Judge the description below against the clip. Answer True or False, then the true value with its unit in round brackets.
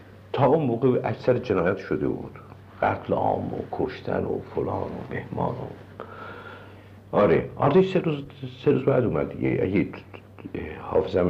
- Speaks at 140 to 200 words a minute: False (125 wpm)